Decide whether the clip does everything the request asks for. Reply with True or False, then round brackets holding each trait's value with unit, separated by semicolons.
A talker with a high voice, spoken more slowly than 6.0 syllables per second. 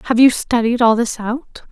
True (235 Hz; 4.8 syllables/s)